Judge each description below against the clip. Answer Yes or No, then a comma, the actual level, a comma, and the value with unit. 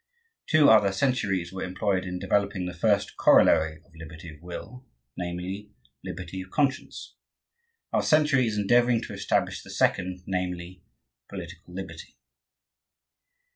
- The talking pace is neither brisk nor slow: No, slow, 130 wpm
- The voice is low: Yes, very low, 95 Hz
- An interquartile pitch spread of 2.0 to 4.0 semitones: Yes, average, 3.0 semitones